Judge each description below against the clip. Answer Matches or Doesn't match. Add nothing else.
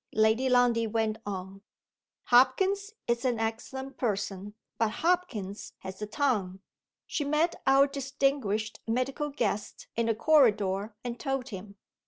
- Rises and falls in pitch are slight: Doesn't match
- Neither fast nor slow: Doesn't match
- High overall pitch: Matches